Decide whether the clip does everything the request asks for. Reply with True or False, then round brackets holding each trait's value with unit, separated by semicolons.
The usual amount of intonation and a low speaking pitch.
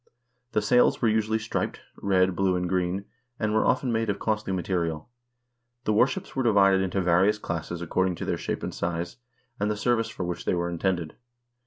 True (3.6 semitones; 95 Hz)